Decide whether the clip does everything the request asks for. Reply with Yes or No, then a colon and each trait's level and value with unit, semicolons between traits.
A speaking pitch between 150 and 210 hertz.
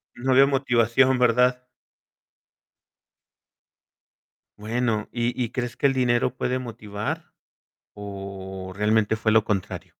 No: low, 115 Hz